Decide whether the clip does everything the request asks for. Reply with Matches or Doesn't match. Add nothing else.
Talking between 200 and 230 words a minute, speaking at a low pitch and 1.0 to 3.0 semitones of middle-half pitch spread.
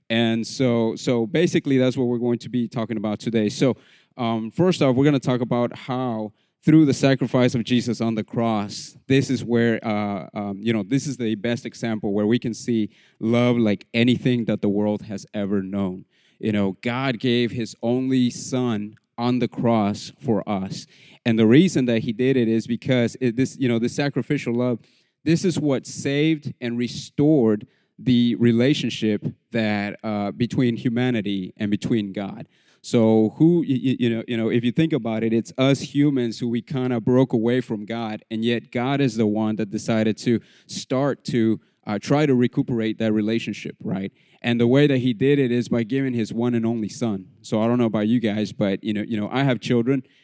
Matches